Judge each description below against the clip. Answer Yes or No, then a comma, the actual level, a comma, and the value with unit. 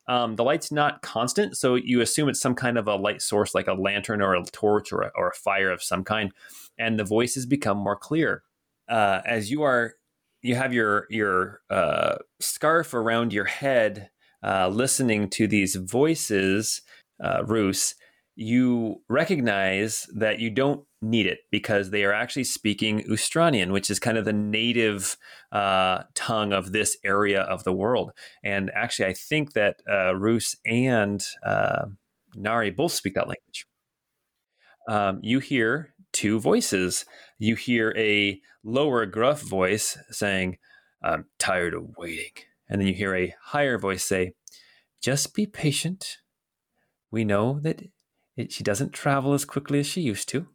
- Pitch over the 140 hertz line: No, low, 110 Hz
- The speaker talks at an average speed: Yes, average, 160 wpm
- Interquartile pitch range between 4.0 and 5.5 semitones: Yes, average, 4.3 semitones